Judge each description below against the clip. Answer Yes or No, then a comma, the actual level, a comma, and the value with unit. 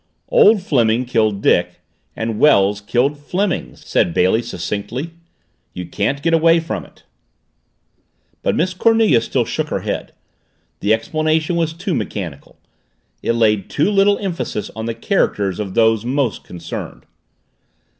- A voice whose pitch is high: No, low, 120 Hz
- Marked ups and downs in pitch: Yes, wide, 8.0 semitones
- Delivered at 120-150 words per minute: Yes, slow, 135 wpm